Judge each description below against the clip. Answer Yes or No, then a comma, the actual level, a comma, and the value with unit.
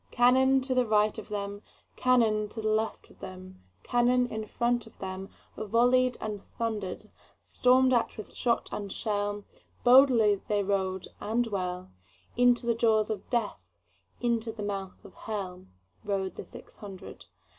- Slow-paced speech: Yes, slow, 120 wpm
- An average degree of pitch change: Yes, average, 3.6 semitones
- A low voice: No, high, 215 Hz